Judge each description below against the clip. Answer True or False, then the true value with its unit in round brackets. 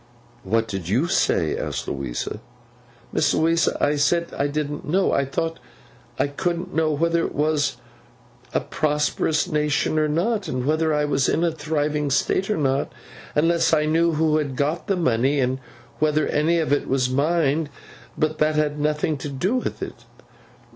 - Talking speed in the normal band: True (170 wpm)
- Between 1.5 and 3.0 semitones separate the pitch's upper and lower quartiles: True (2.4 semitones)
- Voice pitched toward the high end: False (150 Hz)